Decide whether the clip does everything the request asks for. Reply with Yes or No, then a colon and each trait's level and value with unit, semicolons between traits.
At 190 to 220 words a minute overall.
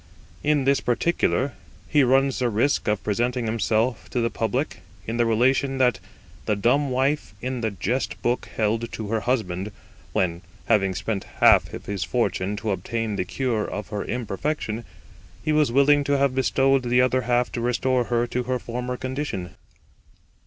No: average, 170 wpm